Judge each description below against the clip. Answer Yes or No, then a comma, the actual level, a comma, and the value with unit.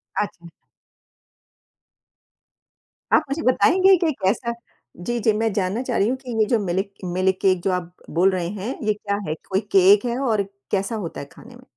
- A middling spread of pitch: Yes, average, 4.3 semitones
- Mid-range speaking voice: No, high, 205 Hz